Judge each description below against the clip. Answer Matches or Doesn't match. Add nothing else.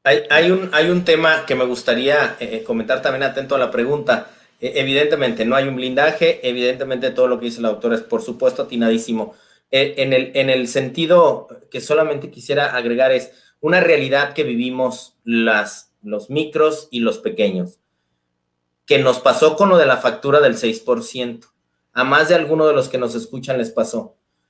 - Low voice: Matches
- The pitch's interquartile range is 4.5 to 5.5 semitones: Matches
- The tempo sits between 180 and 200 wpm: Matches